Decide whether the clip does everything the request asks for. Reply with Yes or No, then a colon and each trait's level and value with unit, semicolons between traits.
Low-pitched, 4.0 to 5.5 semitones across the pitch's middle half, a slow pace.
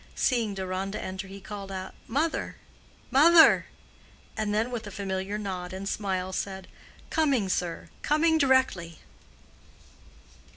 No: high, 200 Hz; average, 5.0 semitones; slow, 115 wpm